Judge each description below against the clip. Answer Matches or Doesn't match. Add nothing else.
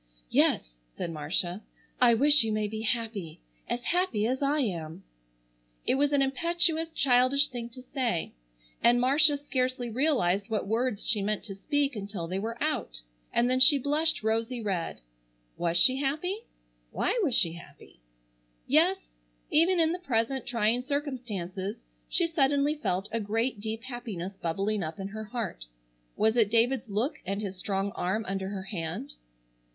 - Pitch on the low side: Doesn't match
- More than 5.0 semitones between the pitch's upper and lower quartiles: Matches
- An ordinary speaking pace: Matches